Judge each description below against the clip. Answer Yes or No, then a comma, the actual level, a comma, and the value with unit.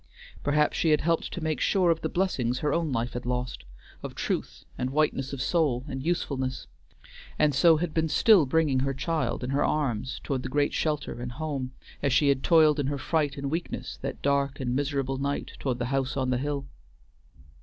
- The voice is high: No, medium, 140 Hz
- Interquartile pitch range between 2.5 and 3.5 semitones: Yes, average, 2.9 semitones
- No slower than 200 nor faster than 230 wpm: Yes, fast, 205 wpm